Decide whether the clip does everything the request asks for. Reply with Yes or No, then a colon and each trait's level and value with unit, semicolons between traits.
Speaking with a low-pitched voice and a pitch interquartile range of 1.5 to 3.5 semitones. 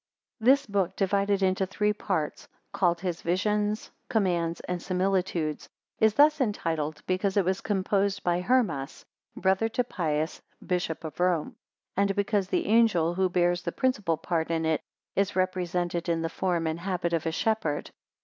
No: medium, 185 Hz; average, 3.1 semitones